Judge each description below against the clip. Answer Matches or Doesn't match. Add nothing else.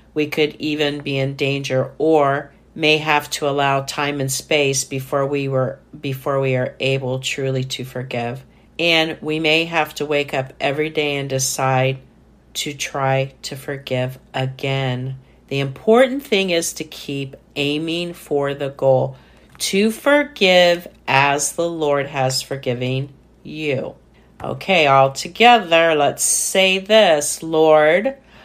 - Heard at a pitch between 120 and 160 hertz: Matches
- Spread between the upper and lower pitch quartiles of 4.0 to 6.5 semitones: Doesn't match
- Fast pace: Doesn't match